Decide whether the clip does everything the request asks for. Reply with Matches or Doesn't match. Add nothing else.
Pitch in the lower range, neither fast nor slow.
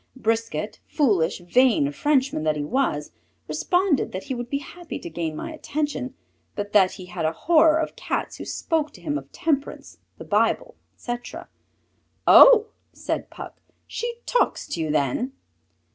Doesn't match